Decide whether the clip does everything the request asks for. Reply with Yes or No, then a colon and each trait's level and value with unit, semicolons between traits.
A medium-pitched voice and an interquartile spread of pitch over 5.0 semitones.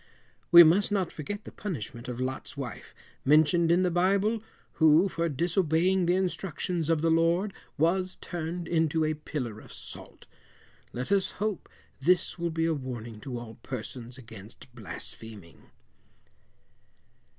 Yes: medium, 165 Hz; wide, 5.5 semitones